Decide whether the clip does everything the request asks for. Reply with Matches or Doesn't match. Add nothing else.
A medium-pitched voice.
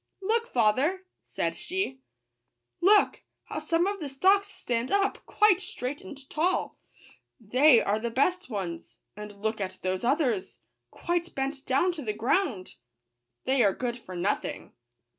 Doesn't match